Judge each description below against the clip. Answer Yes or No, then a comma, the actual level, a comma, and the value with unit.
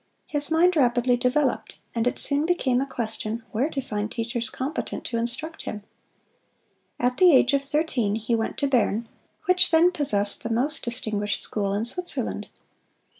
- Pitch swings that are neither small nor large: Yes, average, 4.6 semitones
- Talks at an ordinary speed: Yes, average, 165 wpm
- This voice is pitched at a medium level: No, very high, 250 Hz